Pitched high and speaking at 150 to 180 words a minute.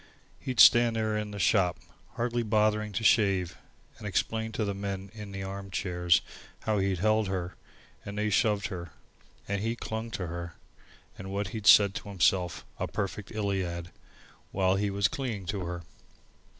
No: low, 100 Hz; average, 170 wpm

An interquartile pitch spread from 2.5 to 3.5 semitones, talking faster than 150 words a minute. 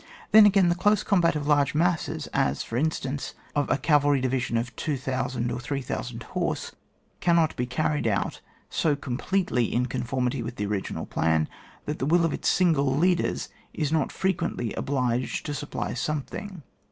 No: average, 5.0 semitones; average, 170 wpm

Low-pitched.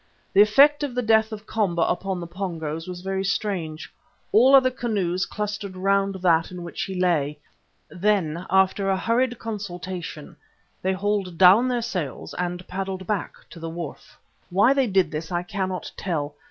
No: high, 190 Hz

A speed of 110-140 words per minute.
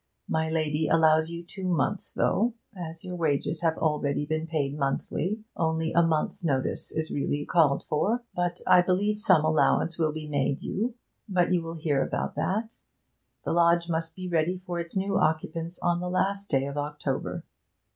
No: average, 175 wpm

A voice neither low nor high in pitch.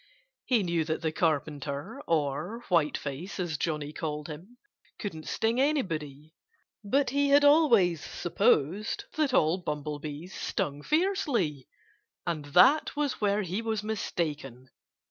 Yes: medium, 170 Hz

